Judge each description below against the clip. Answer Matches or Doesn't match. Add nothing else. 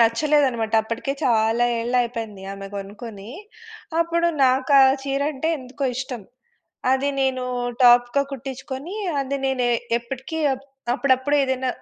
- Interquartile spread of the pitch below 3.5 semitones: Matches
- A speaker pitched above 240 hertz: Matches